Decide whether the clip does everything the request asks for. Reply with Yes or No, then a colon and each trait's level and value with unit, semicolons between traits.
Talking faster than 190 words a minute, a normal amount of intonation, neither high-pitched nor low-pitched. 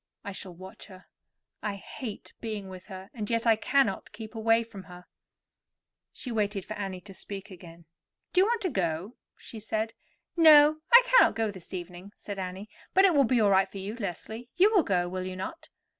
No: fast, 205 wpm; average, 4.1 semitones; high, 205 Hz